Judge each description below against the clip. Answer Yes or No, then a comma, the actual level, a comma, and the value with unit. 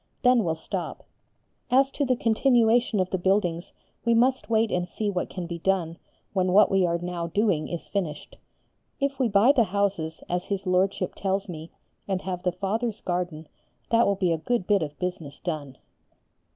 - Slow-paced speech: No, average, 185 wpm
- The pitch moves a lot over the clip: No, average, 4.2 semitones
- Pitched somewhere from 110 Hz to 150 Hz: No, high, 190 Hz